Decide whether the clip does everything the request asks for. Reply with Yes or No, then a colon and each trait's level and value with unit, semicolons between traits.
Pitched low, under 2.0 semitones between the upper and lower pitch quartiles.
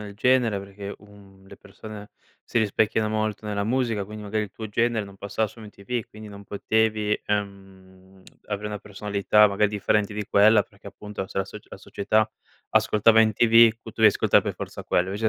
Yes: low, 105 Hz; narrow, 1.5 semitones